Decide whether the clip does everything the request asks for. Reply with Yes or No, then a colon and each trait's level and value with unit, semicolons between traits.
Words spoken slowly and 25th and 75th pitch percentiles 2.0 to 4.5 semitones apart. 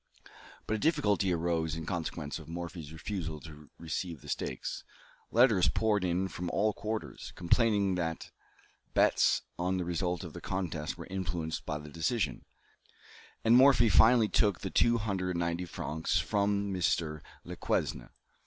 No: average, 150 wpm; average, 3.9 semitones